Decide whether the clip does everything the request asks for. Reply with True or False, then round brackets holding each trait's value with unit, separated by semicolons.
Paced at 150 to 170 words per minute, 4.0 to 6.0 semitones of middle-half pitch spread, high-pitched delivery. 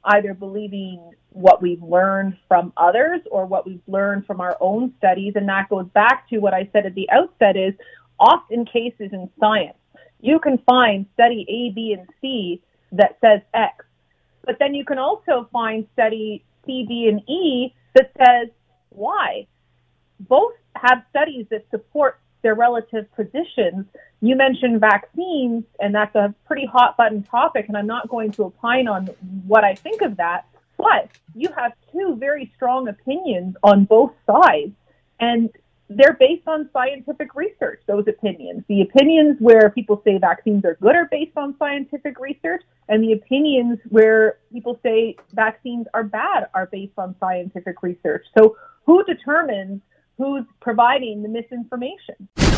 True (155 wpm; 4.8 semitones; 230 Hz)